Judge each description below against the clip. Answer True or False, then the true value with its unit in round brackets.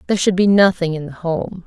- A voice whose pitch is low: False (180 Hz)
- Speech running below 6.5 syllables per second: True (6.0 syllables/s)